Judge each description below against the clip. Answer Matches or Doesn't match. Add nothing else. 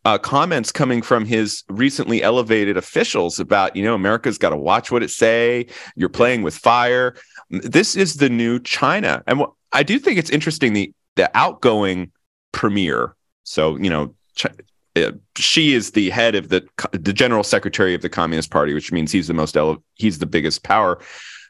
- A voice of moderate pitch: Doesn't match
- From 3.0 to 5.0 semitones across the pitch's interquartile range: Doesn't match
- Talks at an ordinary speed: Matches